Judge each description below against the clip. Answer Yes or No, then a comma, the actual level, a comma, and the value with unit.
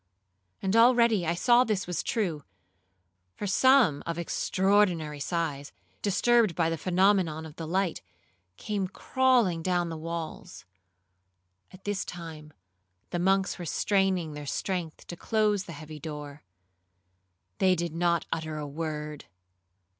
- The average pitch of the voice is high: No, medium, 175 Hz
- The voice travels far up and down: No, average, 3.8 semitones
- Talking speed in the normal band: No, slow, 130 wpm